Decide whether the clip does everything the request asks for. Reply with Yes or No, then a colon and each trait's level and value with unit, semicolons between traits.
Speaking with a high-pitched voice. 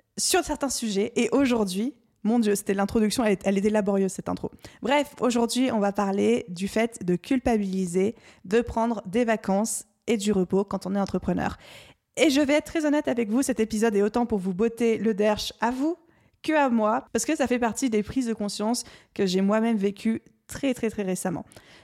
Yes: high, 225 Hz